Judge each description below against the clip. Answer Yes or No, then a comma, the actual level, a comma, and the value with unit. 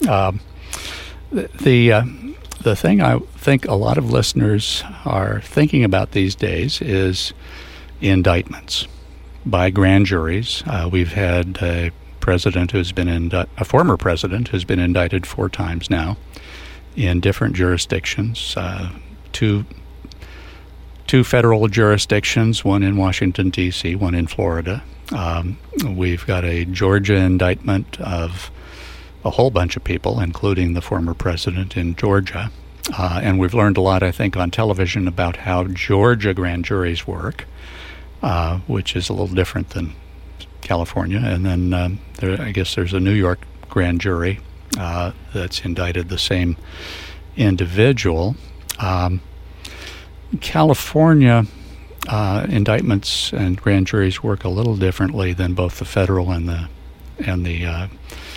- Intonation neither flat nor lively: Yes, average, 3.0 semitones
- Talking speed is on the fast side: No, average, 140 wpm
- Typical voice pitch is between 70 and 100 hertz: Yes, very low, 90 Hz